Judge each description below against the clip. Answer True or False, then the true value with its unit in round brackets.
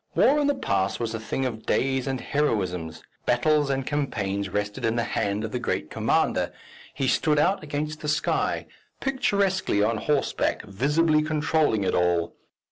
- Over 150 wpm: True (165 wpm)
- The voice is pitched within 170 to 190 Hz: False (135 Hz)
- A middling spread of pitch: False (6.7 semitones)